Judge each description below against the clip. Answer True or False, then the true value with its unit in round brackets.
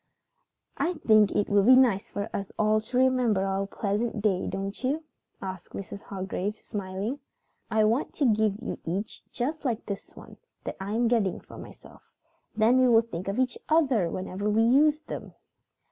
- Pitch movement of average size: True (4.0 semitones)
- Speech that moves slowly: False (180 wpm)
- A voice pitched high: True (215 Hz)